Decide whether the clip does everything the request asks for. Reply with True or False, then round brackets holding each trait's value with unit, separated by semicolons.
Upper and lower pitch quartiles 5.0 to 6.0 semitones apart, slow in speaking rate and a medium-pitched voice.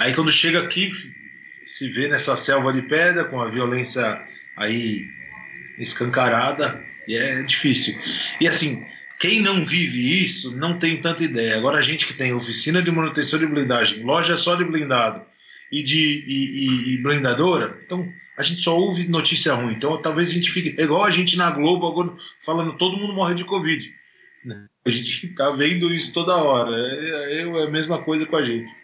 False (5.6 semitones; 180 wpm; 155 Hz)